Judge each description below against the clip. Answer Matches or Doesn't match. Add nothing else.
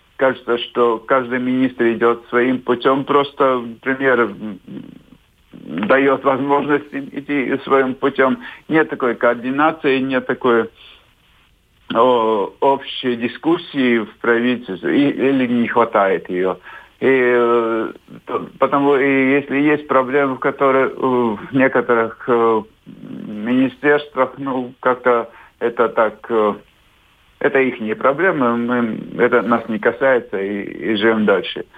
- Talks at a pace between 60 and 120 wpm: Matches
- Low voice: Matches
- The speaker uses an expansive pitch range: Doesn't match